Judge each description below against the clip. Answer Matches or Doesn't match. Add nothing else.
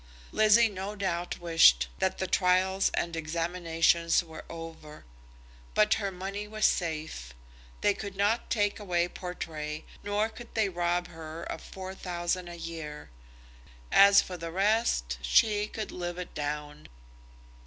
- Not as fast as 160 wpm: Matches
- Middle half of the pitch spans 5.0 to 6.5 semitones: Doesn't match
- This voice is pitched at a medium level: Matches